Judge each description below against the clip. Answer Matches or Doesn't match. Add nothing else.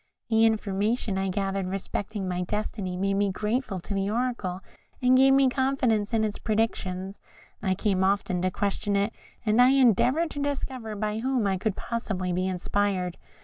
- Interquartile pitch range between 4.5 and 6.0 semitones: Doesn't match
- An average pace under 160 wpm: Doesn't match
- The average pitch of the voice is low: Doesn't match